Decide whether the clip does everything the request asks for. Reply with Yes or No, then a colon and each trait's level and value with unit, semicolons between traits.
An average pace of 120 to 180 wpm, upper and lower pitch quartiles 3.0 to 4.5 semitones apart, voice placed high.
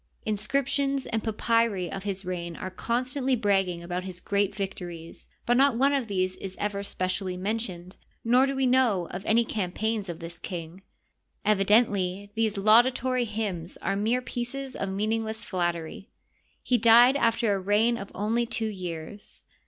Yes: average, 160 wpm; average, 4.1 semitones; high, 210 Hz